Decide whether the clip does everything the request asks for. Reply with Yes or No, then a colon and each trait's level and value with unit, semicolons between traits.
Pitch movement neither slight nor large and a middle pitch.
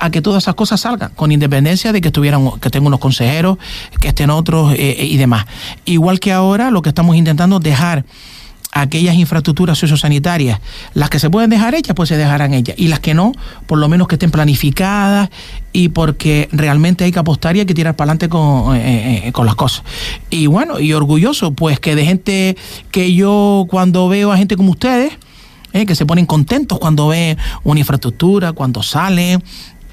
Yes: average, 4.1 semitones; medium, 165 Hz